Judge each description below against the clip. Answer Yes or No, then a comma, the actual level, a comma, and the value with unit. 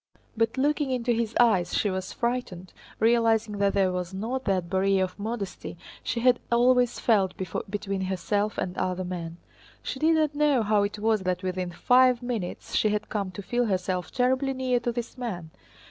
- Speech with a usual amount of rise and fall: Yes, average, 4.5 semitones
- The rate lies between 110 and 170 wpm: No, average, 180 wpm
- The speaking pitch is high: Yes, high, 215 Hz